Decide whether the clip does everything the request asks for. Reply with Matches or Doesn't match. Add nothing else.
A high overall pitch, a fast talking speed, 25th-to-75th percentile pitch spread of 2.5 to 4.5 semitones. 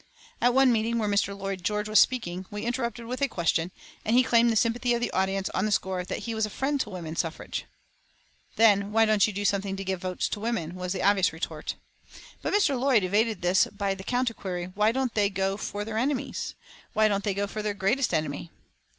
Matches